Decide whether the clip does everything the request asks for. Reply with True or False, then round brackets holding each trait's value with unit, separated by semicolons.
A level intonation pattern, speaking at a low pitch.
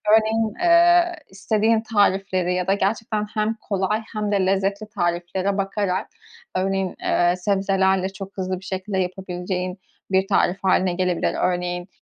False (2.3 semitones; 195 Hz)